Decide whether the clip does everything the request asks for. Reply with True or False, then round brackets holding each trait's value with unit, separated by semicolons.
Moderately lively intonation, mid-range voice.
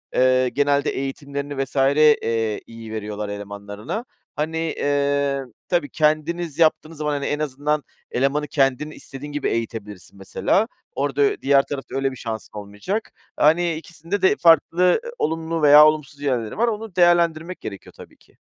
True (4.0 semitones; 145 Hz)